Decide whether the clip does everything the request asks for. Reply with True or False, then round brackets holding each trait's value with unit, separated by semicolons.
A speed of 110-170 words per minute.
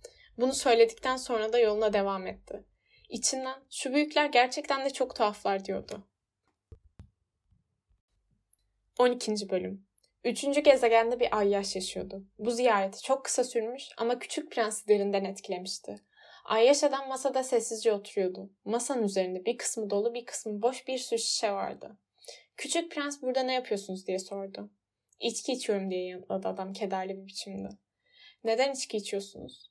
True (135 wpm)